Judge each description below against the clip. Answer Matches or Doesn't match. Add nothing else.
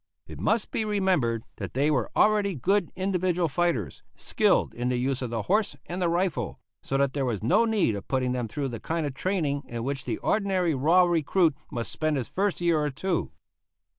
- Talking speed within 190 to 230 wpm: Matches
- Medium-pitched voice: Matches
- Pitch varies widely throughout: Matches